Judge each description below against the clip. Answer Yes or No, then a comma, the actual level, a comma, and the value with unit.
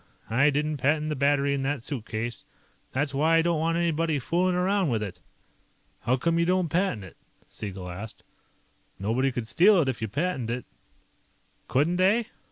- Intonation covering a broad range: Yes, wide, 5.8 semitones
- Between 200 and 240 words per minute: No, average, 175 wpm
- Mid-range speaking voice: Yes, medium, 145 Hz